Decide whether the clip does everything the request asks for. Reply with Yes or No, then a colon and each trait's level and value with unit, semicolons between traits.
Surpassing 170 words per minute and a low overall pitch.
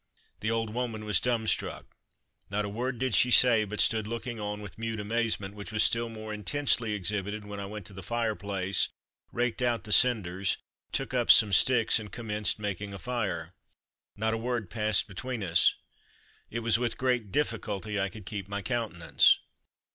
Yes: average, 185 wpm; low, 110 Hz